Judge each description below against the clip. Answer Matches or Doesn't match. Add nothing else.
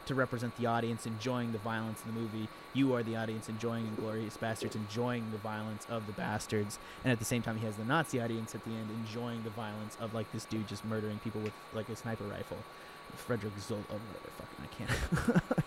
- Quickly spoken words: Matches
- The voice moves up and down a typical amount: Doesn't match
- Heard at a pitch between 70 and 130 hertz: Matches